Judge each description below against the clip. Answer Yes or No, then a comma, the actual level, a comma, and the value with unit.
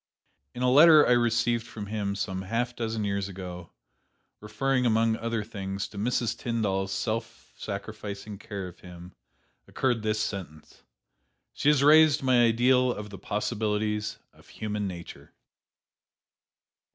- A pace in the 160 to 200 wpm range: No, slow, 135 wpm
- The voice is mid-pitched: No, low, 110 Hz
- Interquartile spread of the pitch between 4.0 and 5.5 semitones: No, average, 3.2 semitones